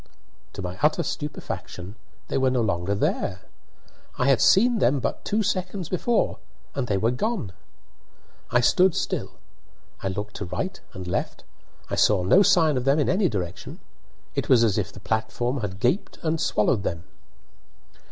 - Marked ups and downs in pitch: Yes, wide, 8.4 semitones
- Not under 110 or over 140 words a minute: No, average, 165 wpm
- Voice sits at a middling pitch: No, low, 125 Hz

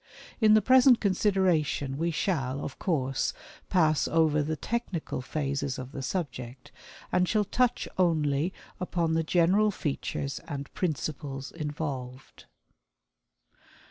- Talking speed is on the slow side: Yes, slow, 115 wpm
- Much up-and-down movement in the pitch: No, average, 5.0 semitones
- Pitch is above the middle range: No, medium, 155 Hz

